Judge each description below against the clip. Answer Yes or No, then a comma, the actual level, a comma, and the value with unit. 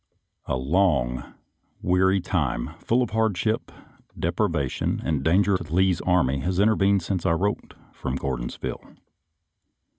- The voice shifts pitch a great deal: Yes, wide, 5.9 semitones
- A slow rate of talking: Yes, slow, 125 wpm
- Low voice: Yes, very low, 90 Hz